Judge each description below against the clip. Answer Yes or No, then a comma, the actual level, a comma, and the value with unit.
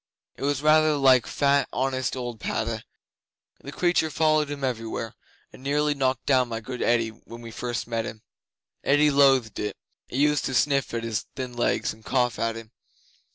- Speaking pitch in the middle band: No, low, 130 Hz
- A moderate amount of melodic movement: Yes, average, 3.7 semitones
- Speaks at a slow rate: No, average, 180 wpm